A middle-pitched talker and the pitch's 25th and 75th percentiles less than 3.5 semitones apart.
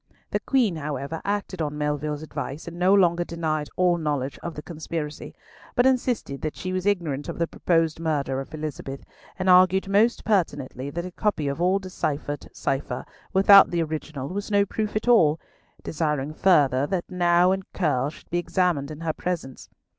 No: medium, 165 Hz; average, 3.9 semitones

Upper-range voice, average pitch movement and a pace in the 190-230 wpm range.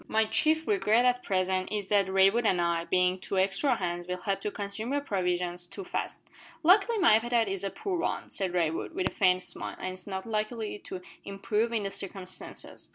Yes: high, 200 Hz; average, 3.7 semitones; fast, 205 wpm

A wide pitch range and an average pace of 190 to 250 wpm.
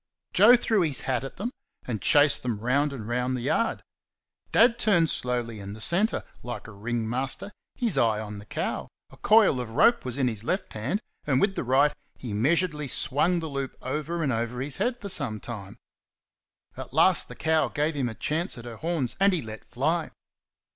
Yes: wide, 6.2 semitones; average, 200 wpm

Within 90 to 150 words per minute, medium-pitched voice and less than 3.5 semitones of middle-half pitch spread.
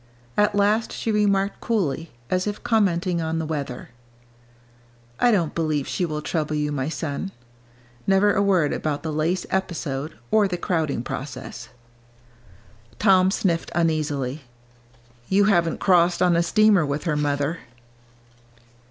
No: slow, 135 wpm; medium, 170 Hz; average, 4.3 semitones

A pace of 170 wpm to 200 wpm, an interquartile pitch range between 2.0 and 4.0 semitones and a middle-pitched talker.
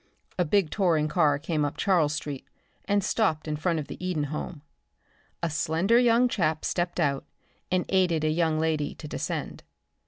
Yes: average, 175 wpm; average, 3.3 semitones; medium, 160 Hz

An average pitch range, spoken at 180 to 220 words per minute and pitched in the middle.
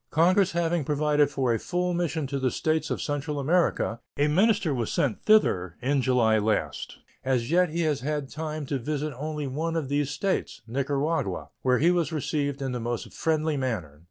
Yes: average, 3.6 semitones; average, 185 wpm; medium, 145 Hz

